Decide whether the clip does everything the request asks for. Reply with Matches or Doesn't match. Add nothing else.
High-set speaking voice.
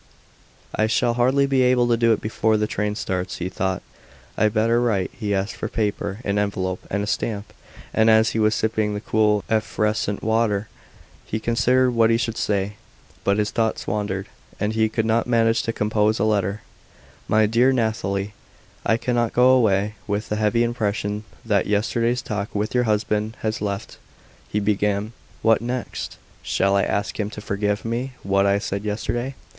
Doesn't match